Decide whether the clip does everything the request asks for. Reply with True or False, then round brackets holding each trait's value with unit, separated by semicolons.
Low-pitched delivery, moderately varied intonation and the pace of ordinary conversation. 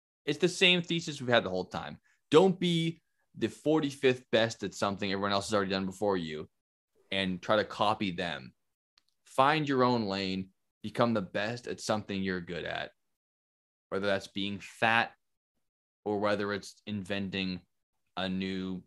True (100 Hz; 4.1 semitones; 160 wpm)